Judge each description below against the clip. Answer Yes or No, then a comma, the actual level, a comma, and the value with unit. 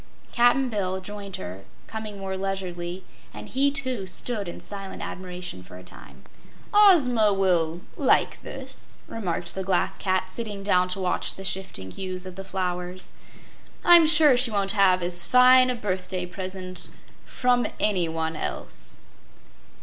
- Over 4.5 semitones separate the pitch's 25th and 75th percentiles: No, average, 3.5 semitones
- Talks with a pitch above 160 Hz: Yes, high, 190 Hz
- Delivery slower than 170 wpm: Yes, average, 145 wpm